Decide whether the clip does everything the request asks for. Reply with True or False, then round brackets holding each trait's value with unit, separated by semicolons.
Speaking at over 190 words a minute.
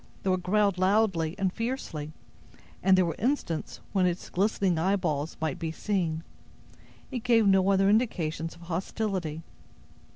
False (140 wpm)